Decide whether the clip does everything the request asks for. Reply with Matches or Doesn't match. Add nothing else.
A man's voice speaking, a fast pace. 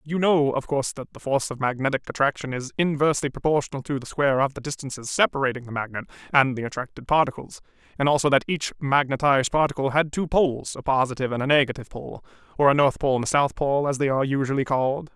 Matches